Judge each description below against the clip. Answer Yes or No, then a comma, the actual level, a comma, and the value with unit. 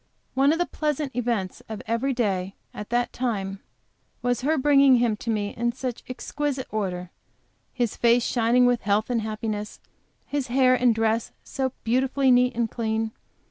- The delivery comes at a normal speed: Yes, average, 165 wpm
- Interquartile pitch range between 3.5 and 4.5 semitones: No, average, 2.9 semitones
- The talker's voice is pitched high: Yes, high, 240 Hz